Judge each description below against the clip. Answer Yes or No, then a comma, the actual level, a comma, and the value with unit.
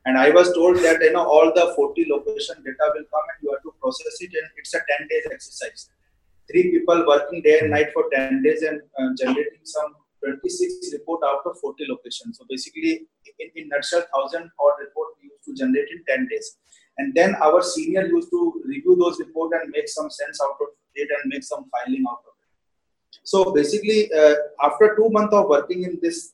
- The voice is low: No, high, 190 Hz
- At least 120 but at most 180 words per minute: No, fast, 205 wpm